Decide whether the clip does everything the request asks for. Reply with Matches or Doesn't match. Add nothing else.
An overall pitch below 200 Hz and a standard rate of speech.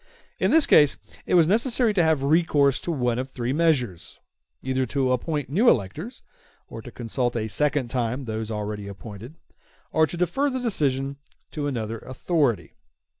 Matches